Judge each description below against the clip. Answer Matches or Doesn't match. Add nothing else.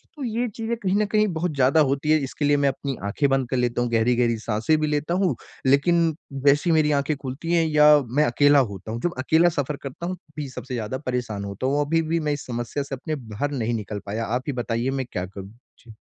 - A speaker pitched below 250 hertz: Matches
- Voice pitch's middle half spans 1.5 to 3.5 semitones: Doesn't match